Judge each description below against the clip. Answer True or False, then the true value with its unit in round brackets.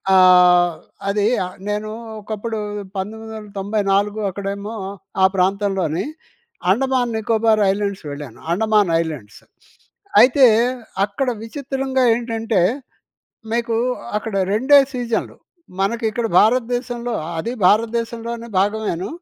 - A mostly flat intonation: False (3.0 semitones)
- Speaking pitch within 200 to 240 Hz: True (215 Hz)